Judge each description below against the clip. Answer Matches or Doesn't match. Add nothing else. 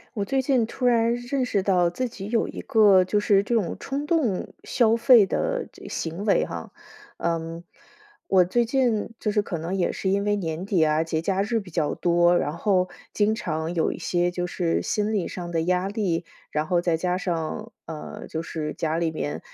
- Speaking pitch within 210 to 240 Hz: Doesn't match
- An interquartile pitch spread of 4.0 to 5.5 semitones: Matches